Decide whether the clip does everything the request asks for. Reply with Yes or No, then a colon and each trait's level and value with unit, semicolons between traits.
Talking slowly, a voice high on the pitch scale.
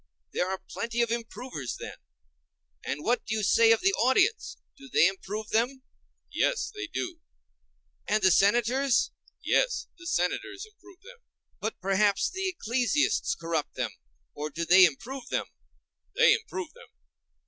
Yes: slow, 125 wpm; high, 235 Hz